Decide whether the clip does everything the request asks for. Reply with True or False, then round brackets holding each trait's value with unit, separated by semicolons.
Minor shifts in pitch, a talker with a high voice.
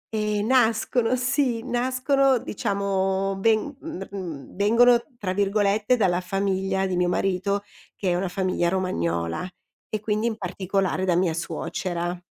False (3.5 semitones; 195 Hz)